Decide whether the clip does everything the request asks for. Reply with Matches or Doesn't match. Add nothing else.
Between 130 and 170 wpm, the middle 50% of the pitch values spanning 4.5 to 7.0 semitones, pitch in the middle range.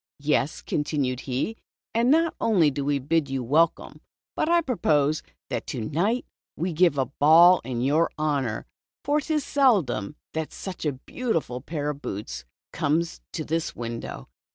Matches